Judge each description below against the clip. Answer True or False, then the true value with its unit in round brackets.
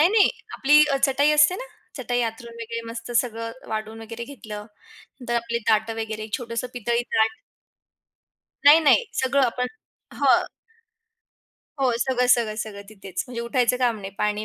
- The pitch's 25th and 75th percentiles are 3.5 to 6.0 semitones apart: False (2.6 semitones)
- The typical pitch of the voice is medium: False (235 Hz)